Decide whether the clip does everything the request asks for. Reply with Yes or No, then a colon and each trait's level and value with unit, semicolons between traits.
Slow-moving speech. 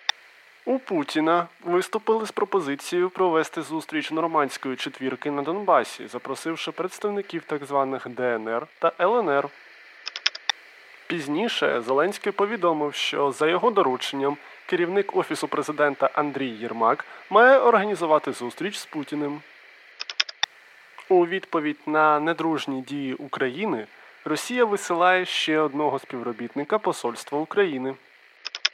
Yes: slow, 100 wpm